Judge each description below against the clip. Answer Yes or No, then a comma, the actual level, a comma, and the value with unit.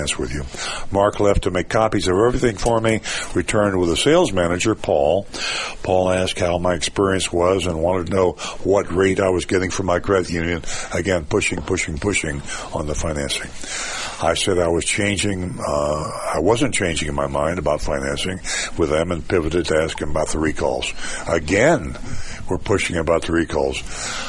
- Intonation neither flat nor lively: Yes, average, 3.2 semitones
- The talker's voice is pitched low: Yes, very low, 90 Hz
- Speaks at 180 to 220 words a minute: Yes, average, 185 wpm